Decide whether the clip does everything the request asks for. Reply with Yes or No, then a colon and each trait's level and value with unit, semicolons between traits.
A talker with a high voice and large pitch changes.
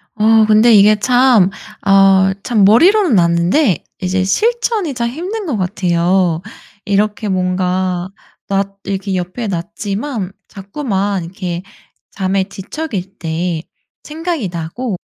No: high, 195 Hz; average, 4.6 semitones